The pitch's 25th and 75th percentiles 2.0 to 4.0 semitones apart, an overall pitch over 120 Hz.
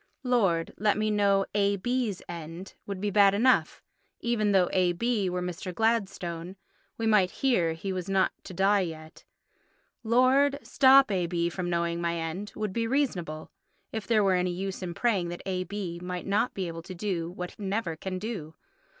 Yes: average, 3.5 semitones; high, 190 Hz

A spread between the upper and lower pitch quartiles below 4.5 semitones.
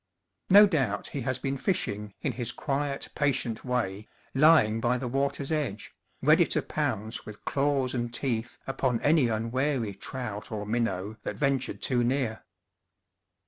Yes: average, 3.8 semitones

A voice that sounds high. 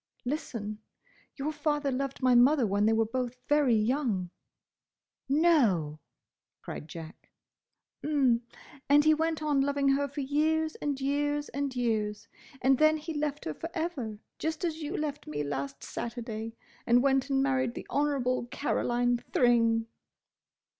Yes: very high, 270 Hz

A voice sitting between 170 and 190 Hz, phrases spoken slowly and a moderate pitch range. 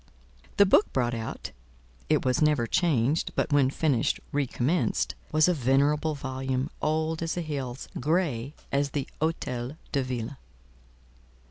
No: medium, 140 Hz; slow, 130 wpm; average, 3.4 semitones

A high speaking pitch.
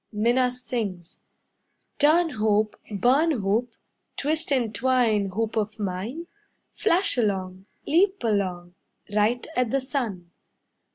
Yes: high, 225 Hz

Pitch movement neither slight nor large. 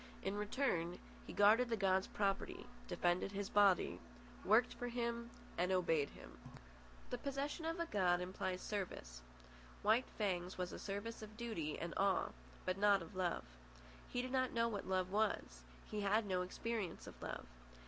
Yes: average, 4.1 semitones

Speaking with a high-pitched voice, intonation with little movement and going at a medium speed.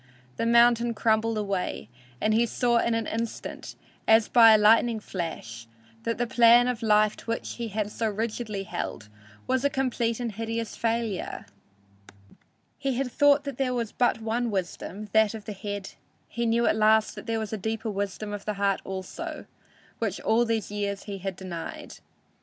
Yes: high, 220 Hz; narrow, 2.3 semitones; average, 175 wpm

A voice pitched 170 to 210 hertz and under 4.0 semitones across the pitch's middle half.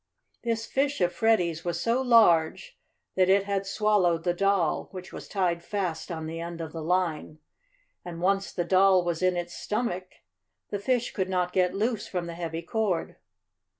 Yes: medium, 185 Hz; average, 3.0 semitones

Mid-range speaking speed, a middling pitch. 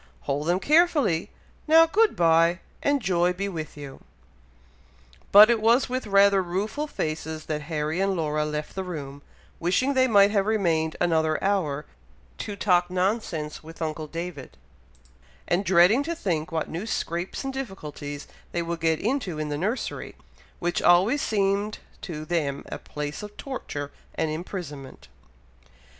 Yes: average, 150 wpm; medium, 175 Hz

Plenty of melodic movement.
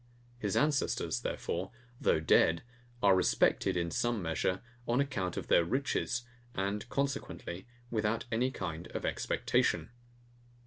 Yes: wide, 5.8 semitones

